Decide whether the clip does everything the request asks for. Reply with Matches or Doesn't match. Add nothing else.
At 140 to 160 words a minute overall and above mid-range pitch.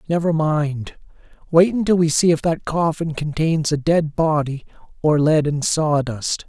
Doesn't match